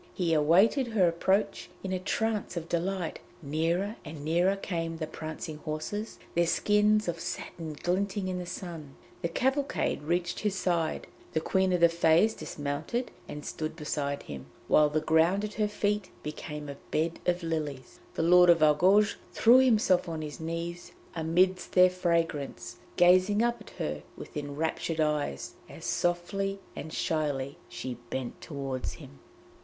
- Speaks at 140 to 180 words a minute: Yes, average, 155 wpm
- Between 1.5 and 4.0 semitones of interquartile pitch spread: Yes, average, 3.7 semitones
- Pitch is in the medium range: Yes, medium, 170 Hz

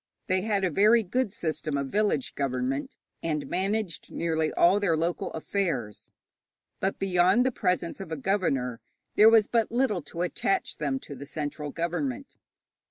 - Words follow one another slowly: No, average, 160 wpm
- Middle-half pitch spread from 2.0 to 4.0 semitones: No, wide, 5.4 semitones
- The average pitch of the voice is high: No, medium, 175 Hz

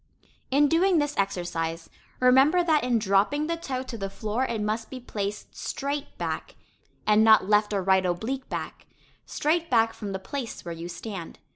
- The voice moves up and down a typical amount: No, wide, 6.2 semitones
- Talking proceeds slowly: No, average, 175 wpm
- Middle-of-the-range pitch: No, high, 225 Hz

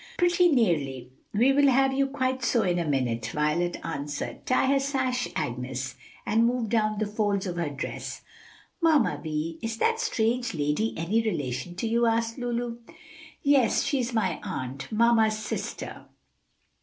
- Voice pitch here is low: No, high, 220 Hz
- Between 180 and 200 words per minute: No, average, 155 wpm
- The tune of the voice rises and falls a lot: Yes, wide, 7.8 semitones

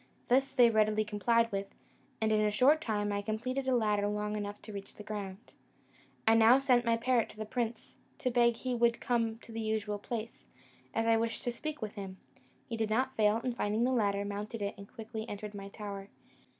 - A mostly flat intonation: Yes, narrow, 2.3 semitones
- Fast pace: Yes, fast, 215 wpm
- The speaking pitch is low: No, high, 220 Hz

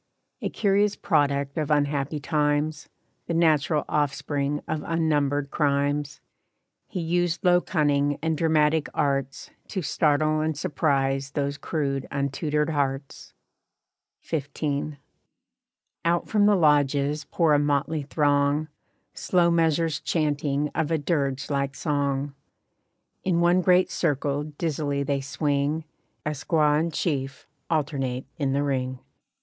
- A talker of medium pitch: Yes, medium, 150 Hz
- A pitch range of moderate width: No, narrow, 2.2 semitones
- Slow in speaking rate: Yes, slow, 120 wpm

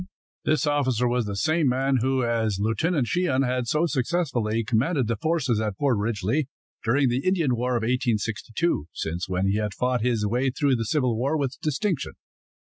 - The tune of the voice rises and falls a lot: No, average, 4.2 semitones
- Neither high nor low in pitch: No, low, 125 Hz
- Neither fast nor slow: Yes, average, 180 wpm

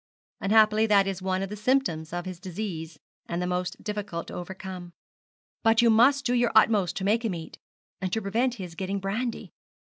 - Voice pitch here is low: No, high, 195 Hz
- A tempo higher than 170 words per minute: Yes, average, 190 wpm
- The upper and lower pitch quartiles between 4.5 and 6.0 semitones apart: No, average, 3.7 semitones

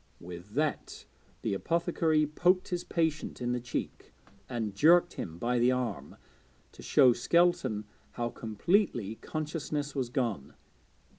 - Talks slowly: Yes, slow, 130 wpm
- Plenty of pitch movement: Yes, wide, 5.9 semitones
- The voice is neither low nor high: No, low, 130 Hz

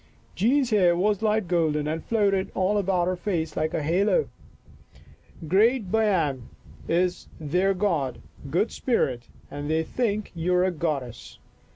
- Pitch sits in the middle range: Yes, medium, 180 Hz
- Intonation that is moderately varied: Yes, average, 4.6 semitones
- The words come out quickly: No, average, 150 wpm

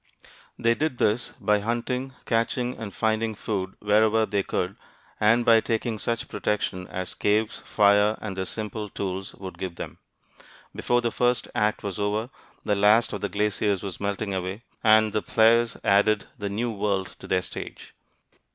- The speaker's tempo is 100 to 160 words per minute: No, average, 170 wpm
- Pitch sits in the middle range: No, low, 105 Hz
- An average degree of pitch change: No, narrow, 2.2 semitones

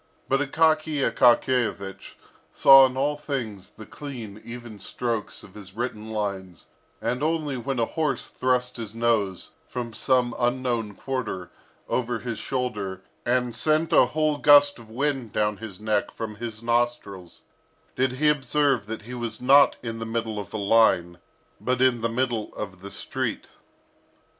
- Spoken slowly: No, average, 155 wpm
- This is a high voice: No, low, 120 Hz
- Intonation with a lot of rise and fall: No, average, 3.5 semitones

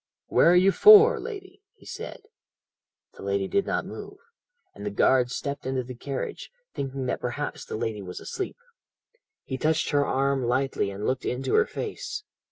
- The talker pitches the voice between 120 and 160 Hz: Yes, low, 135 Hz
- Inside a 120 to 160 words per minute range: No, average, 175 wpm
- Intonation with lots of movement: Yes, wide, 6.5 semitones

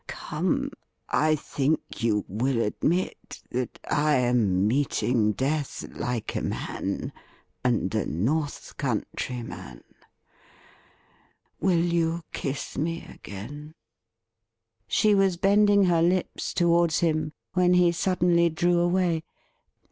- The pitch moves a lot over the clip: Yes, wide, 6.3 semitones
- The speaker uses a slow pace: Yes, slow, 110 wpm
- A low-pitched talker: No, medium, 155 Hz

